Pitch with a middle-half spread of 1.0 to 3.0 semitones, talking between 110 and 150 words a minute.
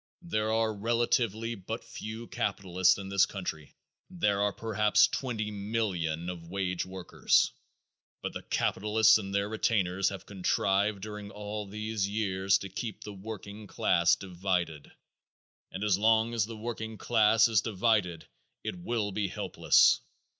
Yes: narrow, 2.6 semitones; average, 140 wpm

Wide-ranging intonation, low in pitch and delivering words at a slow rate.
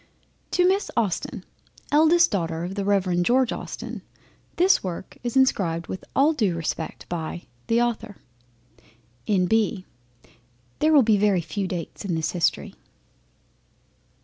No: wide, 5.8 semitones; high, 200 Hz; slow, 130 wpm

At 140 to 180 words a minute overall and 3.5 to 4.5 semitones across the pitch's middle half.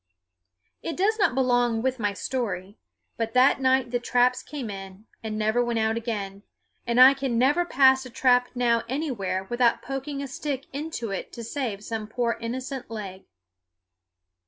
No: average, 165 wpm; average, 3.1 semitones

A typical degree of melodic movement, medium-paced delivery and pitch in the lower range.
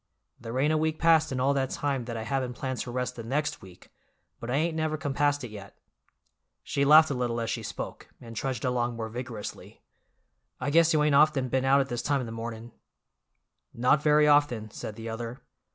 No: average, 3.9 semitones; fast, 215 wpm; low, 130 Hz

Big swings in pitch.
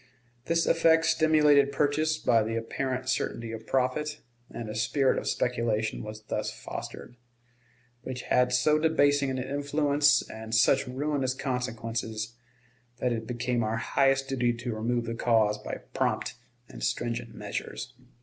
No: average, 3.9 semitones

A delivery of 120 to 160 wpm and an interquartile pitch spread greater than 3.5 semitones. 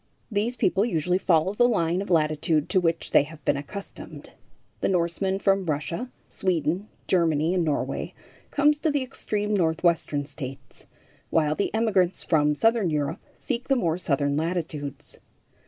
Yes: average, 150 wpm; average, 4.7 semitones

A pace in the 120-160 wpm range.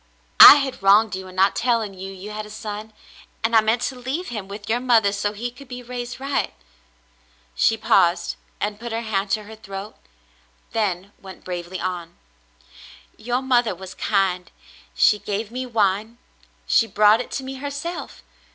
No: average, 180 wpm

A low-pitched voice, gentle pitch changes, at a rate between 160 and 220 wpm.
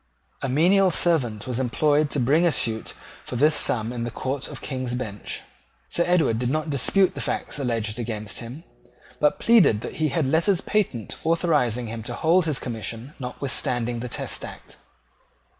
No: low, 130 Hz; average, 5.1 semitones; average, 175 wpm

